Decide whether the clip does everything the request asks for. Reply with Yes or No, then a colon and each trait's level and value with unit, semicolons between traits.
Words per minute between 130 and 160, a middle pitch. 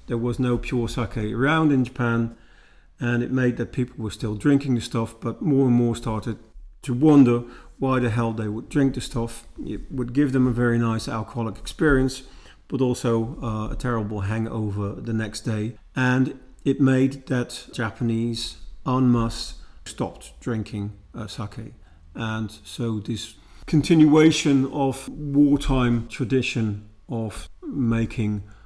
No: average, 150 wpm; low, 120 Hz